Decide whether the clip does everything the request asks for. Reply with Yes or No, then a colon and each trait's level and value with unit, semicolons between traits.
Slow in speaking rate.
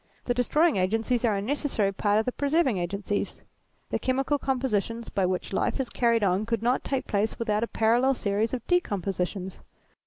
No: average, 180 wpm